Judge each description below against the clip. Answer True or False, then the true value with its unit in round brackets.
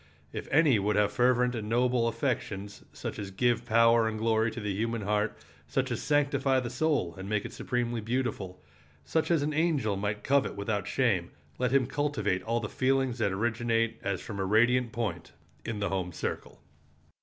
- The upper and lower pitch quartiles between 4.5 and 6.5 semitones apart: False (3.4 semitones)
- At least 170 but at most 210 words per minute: True (185 wpm)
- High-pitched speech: False (115 Hz)